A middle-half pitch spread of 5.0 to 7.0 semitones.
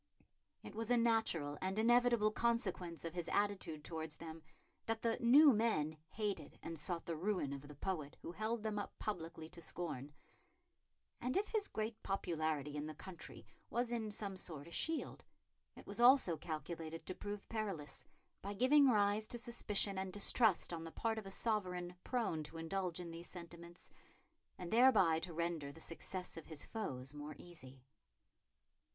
Yes: average, 5.3 semitones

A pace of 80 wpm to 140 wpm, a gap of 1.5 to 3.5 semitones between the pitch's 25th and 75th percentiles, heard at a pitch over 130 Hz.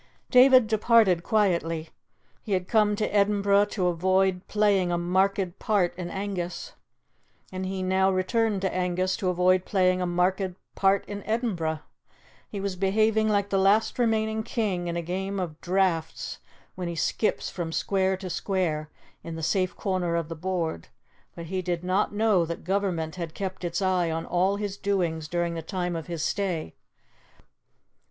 No: average, 165 wpm; narrow, 2.5 semitones; medium, 185 Hz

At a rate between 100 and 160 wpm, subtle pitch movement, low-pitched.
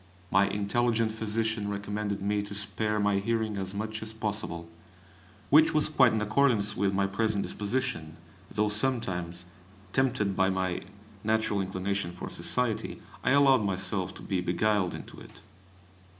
Yes: average, 145 wpm; narrow, 2.3 semitones; low, 105 Hz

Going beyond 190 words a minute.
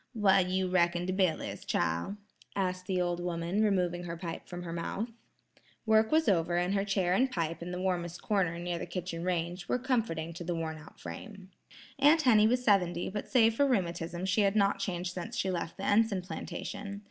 Yes: average, 200 wpm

